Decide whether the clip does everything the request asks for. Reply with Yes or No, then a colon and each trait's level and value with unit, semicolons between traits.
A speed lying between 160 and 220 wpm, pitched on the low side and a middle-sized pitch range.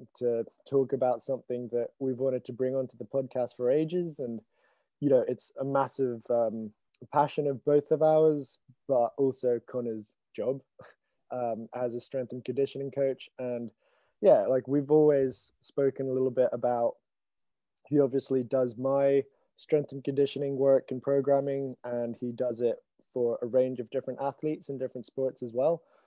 No: average, 165 wpm; low, 130 Hz; narrow, 2.0 semitones